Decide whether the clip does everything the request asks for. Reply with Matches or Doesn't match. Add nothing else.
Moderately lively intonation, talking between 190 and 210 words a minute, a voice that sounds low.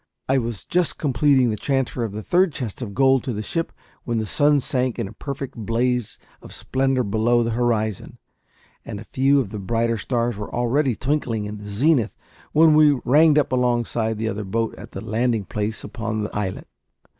Matches